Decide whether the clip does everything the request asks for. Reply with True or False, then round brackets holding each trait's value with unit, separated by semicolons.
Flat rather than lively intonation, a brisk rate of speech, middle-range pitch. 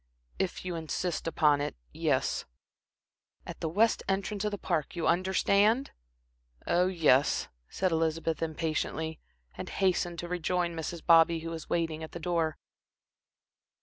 False (2.3 semitones; 140 wpm; 170 Hz)